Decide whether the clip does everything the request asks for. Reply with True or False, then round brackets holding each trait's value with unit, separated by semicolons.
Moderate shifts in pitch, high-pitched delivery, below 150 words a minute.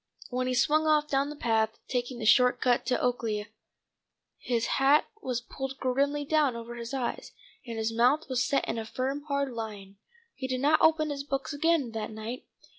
False (3.4 semitones; 255 Hz; 190 wpm)